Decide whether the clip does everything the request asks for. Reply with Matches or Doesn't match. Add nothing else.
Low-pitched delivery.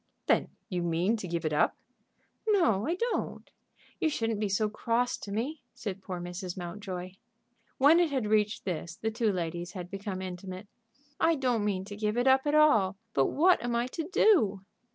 Doesn't match